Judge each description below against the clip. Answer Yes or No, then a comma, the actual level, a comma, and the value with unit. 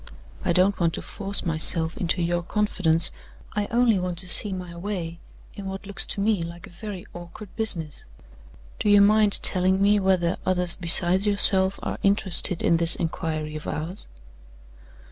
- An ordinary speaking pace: Yes, average, 165 wpm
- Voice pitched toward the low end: No, medium, 185 Hz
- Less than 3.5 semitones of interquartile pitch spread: Yes, average, 2.9 semitones